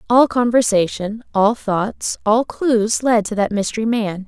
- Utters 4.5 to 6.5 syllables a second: No, 4.1 syllables/s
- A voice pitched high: Yes, high, 220 Hz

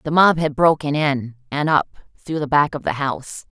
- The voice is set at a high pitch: No, medium, 145 Hz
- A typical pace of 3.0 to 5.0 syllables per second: No, 5.2 syllables/s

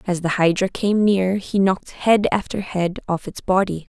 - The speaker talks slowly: No, average, 195 wpm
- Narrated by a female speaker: Yes, female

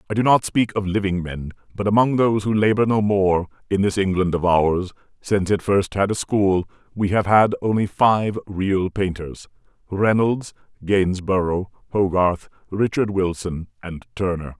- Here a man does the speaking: Yes, male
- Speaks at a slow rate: No, average, 155 wpm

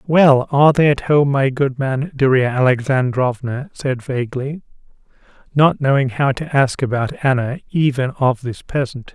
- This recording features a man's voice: Yes, male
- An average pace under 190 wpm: Yes, average, 150 wpm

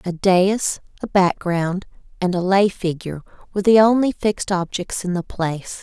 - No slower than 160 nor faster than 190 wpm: Yes, average, 165 wpm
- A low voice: No, medium, 185 Hz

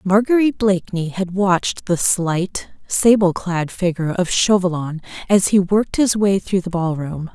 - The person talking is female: Yes, female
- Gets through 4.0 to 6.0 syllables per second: Yes, 4.7 syllables/s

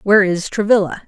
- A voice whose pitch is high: Yes, high, 195 Hz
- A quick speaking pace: No, average, 170 wpm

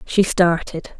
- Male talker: No, female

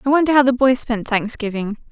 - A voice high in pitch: Yes, high, 240 Hz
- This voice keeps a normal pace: No, fast, 220 wpm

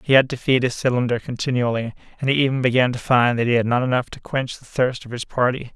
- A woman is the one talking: No, male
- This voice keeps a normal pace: No, fast, 260 wpm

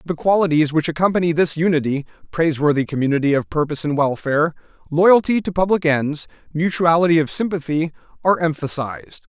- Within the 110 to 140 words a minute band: Yes, slow, 135 wpm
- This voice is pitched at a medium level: Yes, medium, 160 Hz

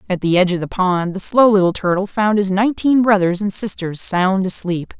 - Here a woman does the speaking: Yes, female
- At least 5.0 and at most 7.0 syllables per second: Yes, 5.4 syllables/s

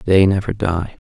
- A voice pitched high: No, very low, 95 Hz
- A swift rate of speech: No, average, 165 wpm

